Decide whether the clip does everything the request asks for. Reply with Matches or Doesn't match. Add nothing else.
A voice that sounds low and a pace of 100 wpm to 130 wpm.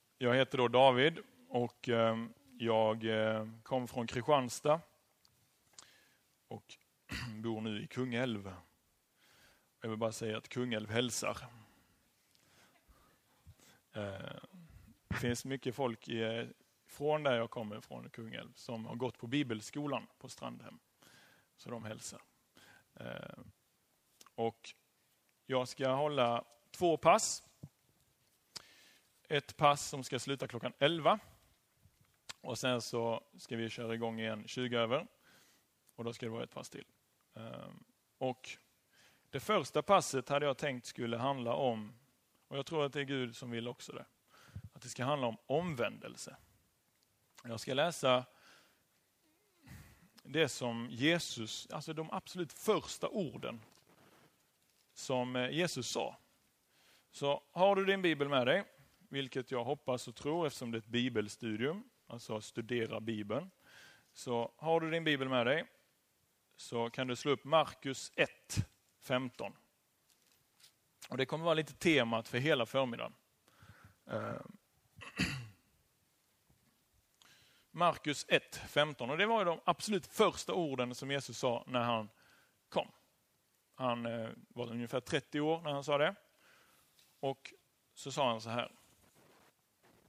Matches